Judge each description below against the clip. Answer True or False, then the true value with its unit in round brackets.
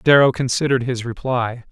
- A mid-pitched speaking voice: False (125 Hz)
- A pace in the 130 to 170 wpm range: True (140 wpm)